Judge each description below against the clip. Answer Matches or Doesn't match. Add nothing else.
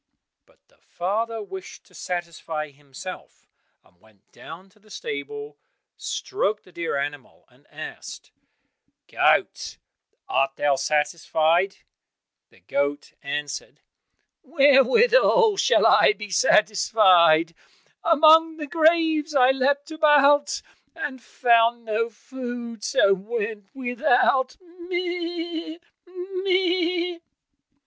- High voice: Matches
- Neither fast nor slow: Doesn't match